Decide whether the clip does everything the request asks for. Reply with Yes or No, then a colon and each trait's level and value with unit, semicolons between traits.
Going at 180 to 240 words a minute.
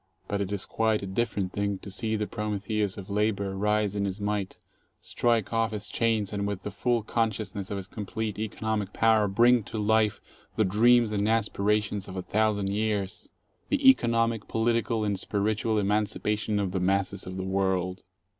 Yes: average, 185 wpm